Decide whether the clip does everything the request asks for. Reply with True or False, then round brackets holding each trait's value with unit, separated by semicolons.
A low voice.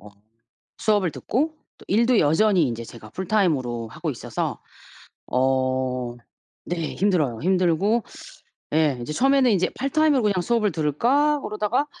False (185 Hz)